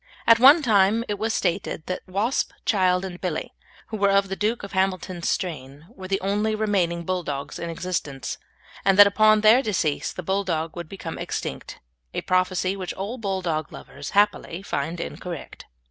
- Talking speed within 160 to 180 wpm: Yes, average, 170 wpm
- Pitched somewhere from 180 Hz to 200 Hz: Yes, high, 190 Hz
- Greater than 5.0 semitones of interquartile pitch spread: No, average, 3.2 semitones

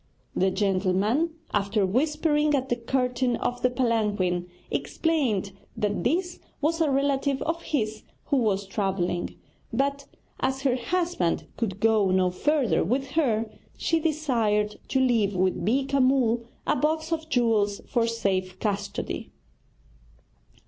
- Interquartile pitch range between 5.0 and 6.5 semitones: Yes, wide, 5.6 semitones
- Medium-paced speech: No, slow, 130 wpm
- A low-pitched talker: No, high, 240 Hz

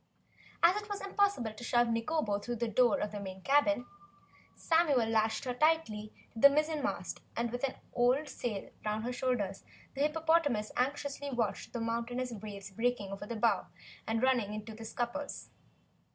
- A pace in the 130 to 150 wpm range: No, average, 170 wpm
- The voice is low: No, high, 240 Hz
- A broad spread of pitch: No, average, 4.8 semitones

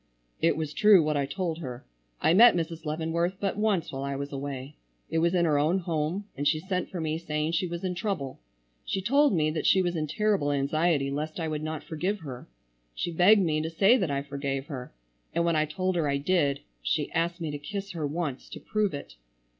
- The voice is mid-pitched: Yes, medium, 160 Hz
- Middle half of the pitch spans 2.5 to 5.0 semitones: Yes, average, 3.9 semitones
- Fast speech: Yes, fast, 225 wpm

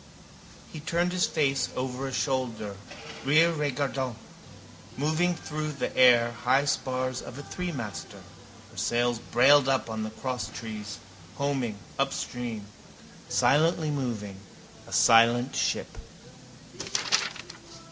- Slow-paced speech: Yes, slow, 105 wpm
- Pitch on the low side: Yes, low, 130 Hz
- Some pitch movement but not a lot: Yes, average, 3.6 semitones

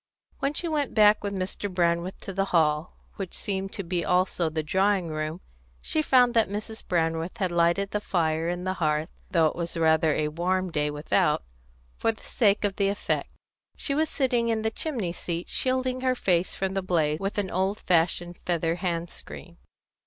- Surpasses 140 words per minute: Yes, average, 195 wpm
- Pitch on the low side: No, medium, 185 Hz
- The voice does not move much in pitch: No, average, 3.7 semitones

